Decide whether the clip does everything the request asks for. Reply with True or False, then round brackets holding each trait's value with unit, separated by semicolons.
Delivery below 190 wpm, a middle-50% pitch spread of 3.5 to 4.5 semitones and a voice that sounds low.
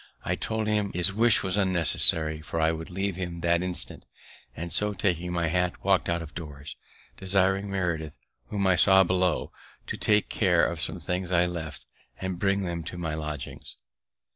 False (180 wpm; 2.5 semitones; 90 Hz)